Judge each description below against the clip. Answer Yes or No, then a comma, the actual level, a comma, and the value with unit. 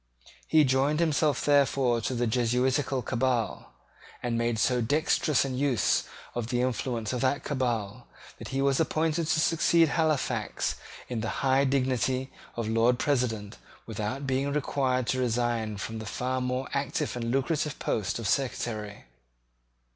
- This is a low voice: Yes, low, 130 Hz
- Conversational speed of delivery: Yes, average, 145 wpm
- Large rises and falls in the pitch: No, average, 3.0 semitones